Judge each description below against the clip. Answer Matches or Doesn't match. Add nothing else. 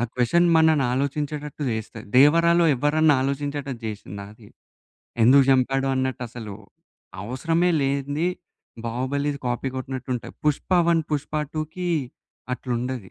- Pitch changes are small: Doesn't match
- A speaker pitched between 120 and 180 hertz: Matches